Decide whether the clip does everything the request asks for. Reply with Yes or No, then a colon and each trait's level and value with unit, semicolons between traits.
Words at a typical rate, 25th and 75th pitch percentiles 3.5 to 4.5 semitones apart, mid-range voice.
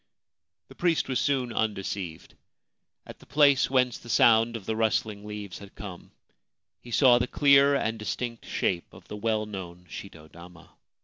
No: average, 165 wpm; average, 4.2 semitones; low, 110 Hz